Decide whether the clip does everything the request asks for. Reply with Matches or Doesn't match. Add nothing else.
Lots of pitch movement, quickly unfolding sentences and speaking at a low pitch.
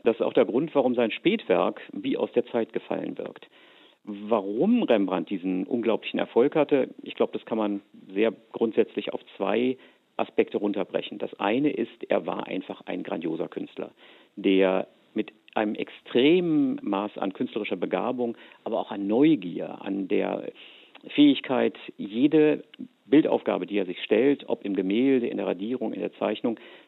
Doesn't match